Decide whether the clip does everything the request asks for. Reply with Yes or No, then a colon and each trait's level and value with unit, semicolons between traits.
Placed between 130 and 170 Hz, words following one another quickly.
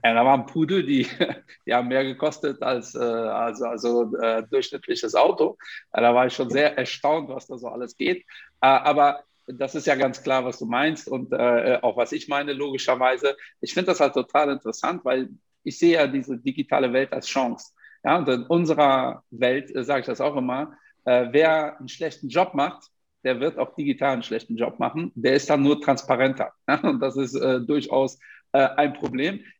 Yes: low, 135 Hz; fast, 195 wpm